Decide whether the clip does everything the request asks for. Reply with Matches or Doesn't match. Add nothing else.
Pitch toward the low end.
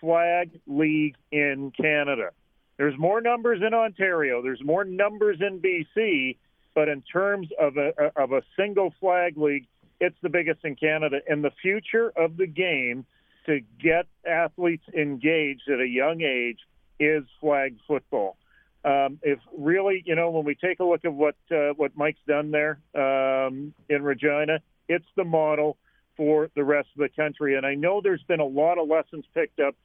Doesn't match